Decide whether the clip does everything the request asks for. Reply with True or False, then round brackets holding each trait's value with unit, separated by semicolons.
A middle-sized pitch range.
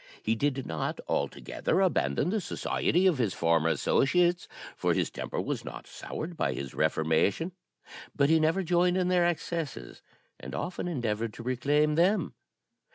False (7.7 semitones)